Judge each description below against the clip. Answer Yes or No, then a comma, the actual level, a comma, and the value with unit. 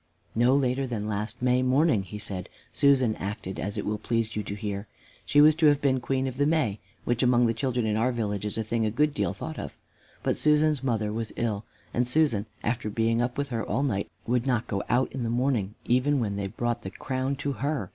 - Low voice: Yes, low, 120 Hz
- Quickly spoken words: Yes, fast, 235 wpm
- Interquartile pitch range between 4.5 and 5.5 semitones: No, average, 3.9 semitones